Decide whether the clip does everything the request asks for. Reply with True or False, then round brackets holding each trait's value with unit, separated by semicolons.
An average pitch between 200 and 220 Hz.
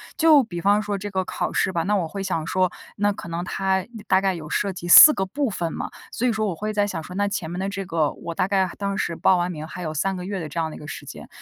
False (190 Hz)